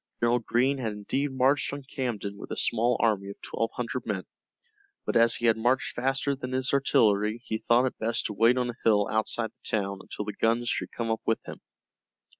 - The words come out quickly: Yes, fast, 215 wpm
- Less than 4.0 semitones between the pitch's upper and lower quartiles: Yes, average, 2.7 semitones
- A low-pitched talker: Yes, low, 115 Hz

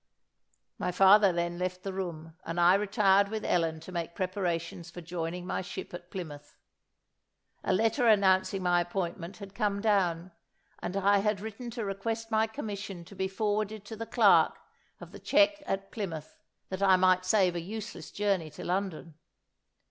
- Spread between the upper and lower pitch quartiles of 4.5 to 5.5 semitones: No, average, 2.9 semitones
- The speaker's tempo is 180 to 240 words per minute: No, average, 170 wpm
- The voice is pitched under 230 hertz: Yes, high, 190 Hz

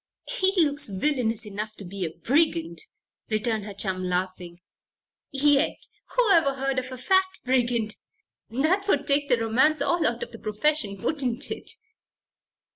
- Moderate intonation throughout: No, wide, 5.7 semitones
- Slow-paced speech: No, average, 145 wpm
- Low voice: No, high, 245 Hz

